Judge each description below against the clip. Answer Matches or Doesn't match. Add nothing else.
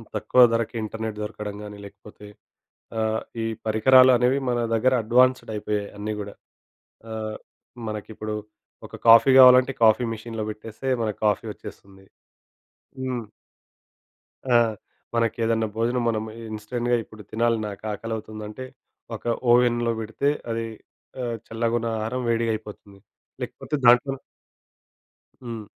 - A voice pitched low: Matches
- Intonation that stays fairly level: Matches